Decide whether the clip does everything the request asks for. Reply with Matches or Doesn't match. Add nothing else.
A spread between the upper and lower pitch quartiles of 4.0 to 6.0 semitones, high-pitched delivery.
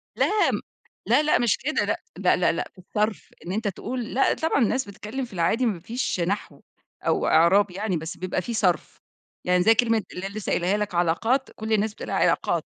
Matches